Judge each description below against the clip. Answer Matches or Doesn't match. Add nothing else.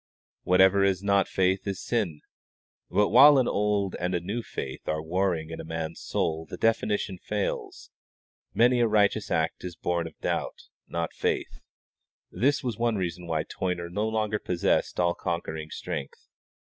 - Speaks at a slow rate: Doesn't match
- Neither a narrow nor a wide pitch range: Matches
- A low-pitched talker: Matches